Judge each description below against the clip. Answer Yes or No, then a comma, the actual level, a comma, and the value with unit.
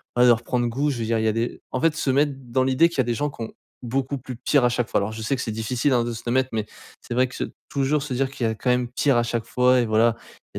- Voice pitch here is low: Yes, low, 125 Hz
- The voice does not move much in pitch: Yes, narrow, 2.2 semitones